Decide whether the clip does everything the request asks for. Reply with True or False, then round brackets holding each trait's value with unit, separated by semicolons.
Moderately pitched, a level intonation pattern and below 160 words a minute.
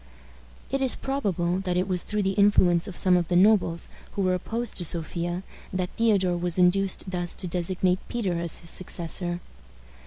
False (180 Hz; 2.1 semitones; 180 wpm)